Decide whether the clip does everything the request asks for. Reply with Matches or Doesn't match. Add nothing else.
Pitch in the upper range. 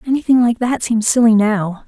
Matches